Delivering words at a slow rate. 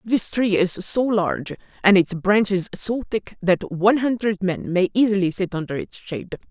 No: average, 185 wpm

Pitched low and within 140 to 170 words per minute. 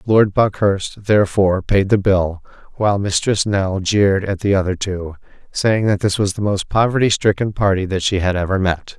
No: low, 100 Hz; average, 185 wpm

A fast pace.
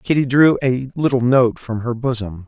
No: average, 195 wpm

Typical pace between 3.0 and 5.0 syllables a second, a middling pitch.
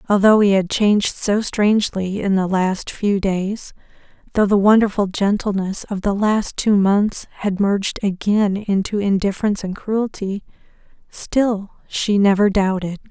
No: 4.4 syllables/s; high, 200 Hz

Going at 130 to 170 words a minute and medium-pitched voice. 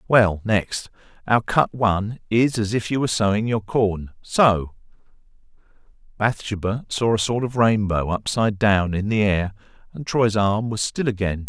No: average, 155 wpm; low, 105 Hz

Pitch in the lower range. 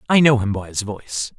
Yes: low, 110 Hz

